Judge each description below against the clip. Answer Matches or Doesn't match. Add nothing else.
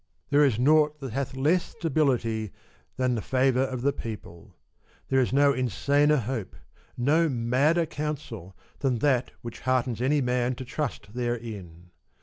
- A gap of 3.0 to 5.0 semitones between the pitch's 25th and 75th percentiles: Matches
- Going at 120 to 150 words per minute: Matches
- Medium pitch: Doesn't match